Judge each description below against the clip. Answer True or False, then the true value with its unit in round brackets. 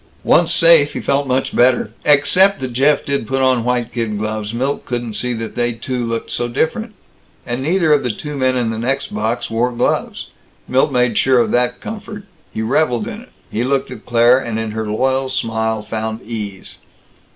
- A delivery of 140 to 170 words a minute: False (195 wpm)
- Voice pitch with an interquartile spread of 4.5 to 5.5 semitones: False (2.9 semitones)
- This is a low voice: True (125 Hz)